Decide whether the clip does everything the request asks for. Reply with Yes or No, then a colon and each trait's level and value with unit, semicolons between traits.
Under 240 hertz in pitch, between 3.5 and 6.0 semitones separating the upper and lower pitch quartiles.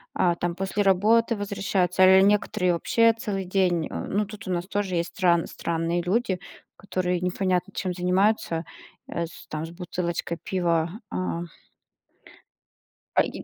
No: medium, 185 Hz; narrow, 2.4 semitones